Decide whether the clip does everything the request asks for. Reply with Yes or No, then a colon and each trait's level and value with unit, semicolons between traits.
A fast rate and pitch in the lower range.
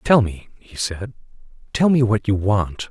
No: average, 165 wpm; low, 105 Hz